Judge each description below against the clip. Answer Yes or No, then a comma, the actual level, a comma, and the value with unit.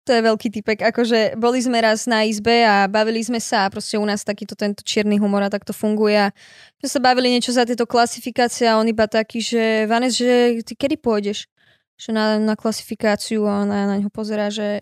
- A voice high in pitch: Yes, high, 220 Hz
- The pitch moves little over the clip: Yes, narrow, 2.2 semitones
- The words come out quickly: Yes, fast, 215 wpm